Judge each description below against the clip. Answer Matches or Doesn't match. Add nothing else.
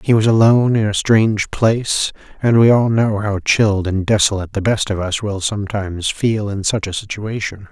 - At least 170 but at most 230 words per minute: Matches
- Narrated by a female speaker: Doesn't match